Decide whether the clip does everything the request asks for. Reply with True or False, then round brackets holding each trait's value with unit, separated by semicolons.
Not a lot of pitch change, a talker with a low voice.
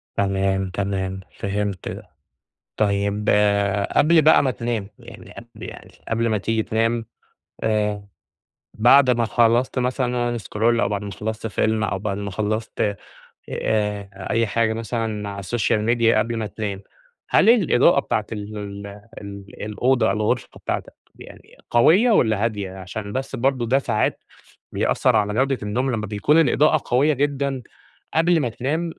False (3.4 semitones; 110 Hz)